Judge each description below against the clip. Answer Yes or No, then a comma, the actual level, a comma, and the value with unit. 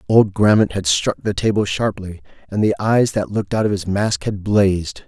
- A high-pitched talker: No, low, 100 Hz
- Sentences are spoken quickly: Yes, fast, 215 wpm